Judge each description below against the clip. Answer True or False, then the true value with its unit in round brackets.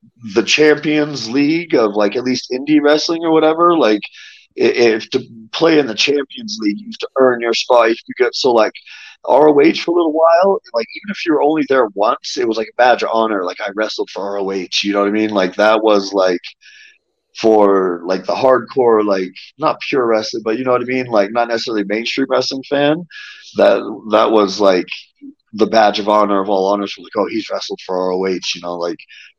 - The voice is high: False (125 Hz)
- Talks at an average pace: False (210 wpm)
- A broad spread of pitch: True (7.3 semitones)